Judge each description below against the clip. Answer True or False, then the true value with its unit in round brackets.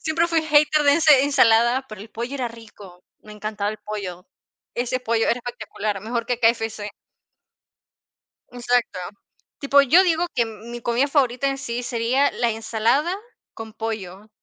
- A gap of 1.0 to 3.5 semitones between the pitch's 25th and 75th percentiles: False (3.9 semitones)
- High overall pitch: True (235 Hz)